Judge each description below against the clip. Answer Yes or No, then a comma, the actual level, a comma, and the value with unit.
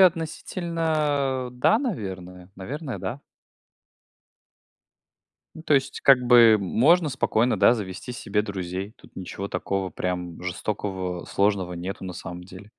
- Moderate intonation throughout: No, wide, 6.6 semitones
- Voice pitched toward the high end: No, low, 105 Hz